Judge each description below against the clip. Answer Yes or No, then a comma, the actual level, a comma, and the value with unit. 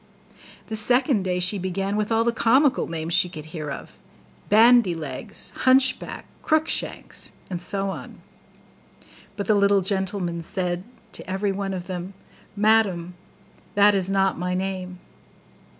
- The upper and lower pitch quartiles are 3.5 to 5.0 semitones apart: No, average, 2.9 semitones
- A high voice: Yes, high, 195 Hz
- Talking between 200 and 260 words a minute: No, average, 150 wpm